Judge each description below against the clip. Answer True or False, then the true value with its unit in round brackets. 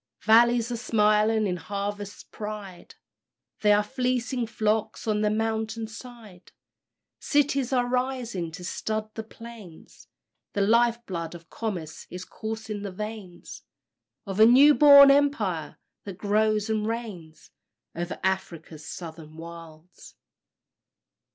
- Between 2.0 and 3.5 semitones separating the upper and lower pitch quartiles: False (4.1 semitones)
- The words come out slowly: True (120 wpm)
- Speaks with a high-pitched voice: True (215 Hz)